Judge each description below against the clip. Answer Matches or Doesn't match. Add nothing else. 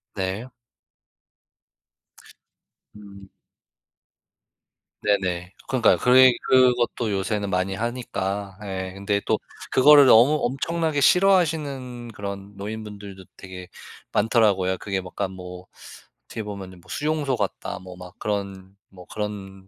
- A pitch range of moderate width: Matches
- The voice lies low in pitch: Matches